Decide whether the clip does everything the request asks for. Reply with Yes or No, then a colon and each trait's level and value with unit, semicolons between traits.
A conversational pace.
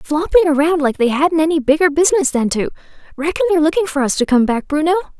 No: fast, 210 wpm